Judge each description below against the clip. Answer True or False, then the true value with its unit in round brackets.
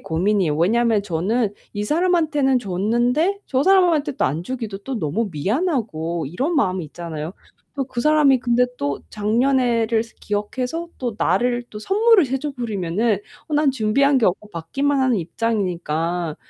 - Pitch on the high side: True (230 Hz)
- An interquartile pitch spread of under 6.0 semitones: False (6.9 semitones)